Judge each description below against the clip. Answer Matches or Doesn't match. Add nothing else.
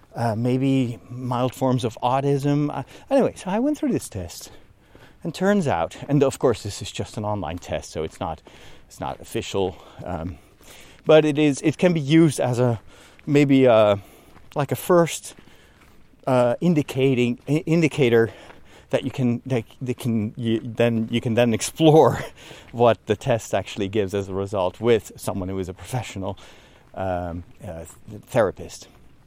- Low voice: Matches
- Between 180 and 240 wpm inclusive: Doesn't match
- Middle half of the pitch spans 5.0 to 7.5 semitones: Matches